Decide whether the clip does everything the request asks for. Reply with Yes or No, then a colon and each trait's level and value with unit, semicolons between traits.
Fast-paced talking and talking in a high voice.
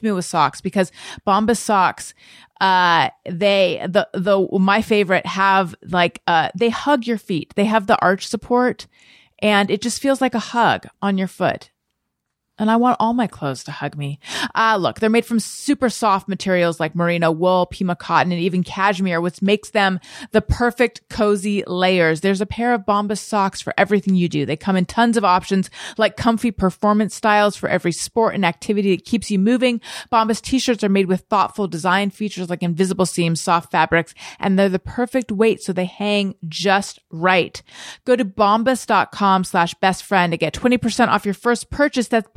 No: average, 190 wpm; high, 200 Hz